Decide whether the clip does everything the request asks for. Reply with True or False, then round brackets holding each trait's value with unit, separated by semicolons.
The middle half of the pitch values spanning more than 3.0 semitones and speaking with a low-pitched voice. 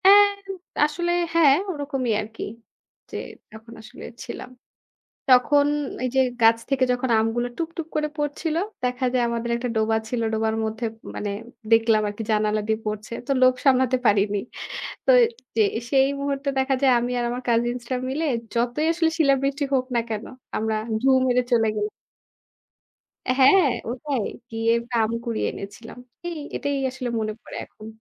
False (3.9 semitones; 250 Hz)